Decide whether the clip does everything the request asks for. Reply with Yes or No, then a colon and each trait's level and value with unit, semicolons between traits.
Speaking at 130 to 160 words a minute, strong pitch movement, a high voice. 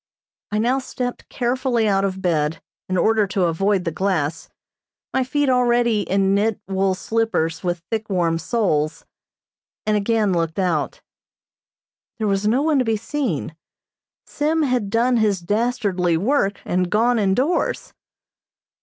No: average, 145 wpm; average, 4.7 semitones; high, 205 Hz